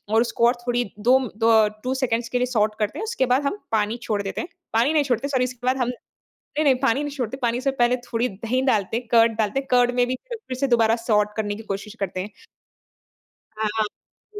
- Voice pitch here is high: Yes, high, 240 Hz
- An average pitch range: Yes, average, 3.0 semitones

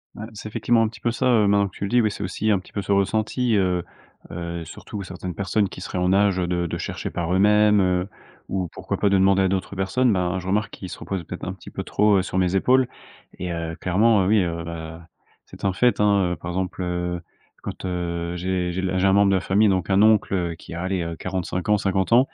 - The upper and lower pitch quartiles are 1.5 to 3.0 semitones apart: Yes, narrow, 2.5 semitones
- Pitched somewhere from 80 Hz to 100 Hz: Yes, very low, 95 Hz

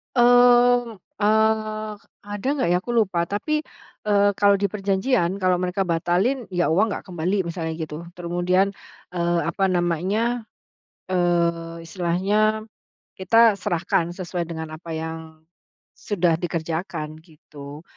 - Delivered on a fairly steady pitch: No, average, 3.5 semitones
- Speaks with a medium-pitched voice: Yes, medium, 180 Hz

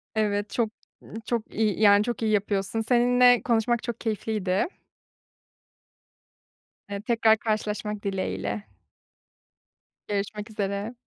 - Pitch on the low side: No, high, 215 Hz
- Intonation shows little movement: Yes, narrow, 2.1 semitones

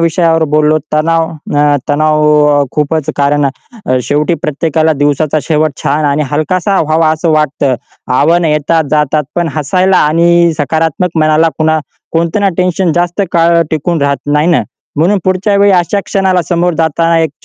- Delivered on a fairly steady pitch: Yes, narrow, 2.3 semitones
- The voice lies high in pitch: No, medium, 160 Hz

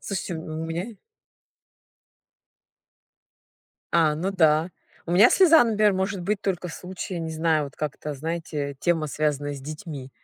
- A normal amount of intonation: Yes, average, 3.7 semitones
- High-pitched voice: No, medium, 165 Hz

